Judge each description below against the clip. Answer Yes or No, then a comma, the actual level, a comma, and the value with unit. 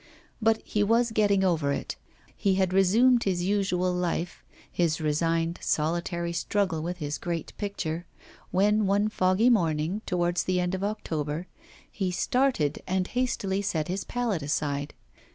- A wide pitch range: No, average, 3.6 semitones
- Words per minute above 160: No, average, 145 wpm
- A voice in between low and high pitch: Yes, medium, 180 Hz